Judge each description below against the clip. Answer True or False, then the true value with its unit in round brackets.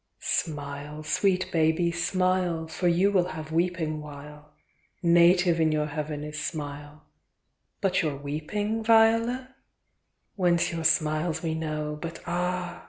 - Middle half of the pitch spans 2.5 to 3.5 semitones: True (3.0 semitones)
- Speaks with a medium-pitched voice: True (165 Hz)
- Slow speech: True (130 wpm)